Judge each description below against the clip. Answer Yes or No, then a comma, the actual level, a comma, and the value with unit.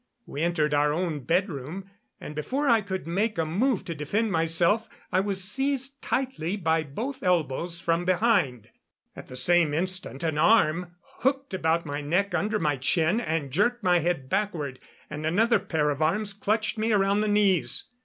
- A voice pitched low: No, medium, 180 Hz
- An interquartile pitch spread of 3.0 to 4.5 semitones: No, average, 5.1 semitones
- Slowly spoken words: No, average, 175 wpm